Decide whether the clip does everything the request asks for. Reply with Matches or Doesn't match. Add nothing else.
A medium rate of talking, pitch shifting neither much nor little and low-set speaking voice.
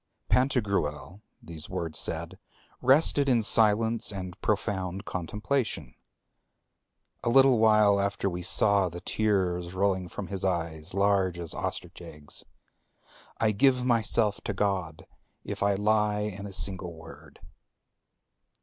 Doesn't match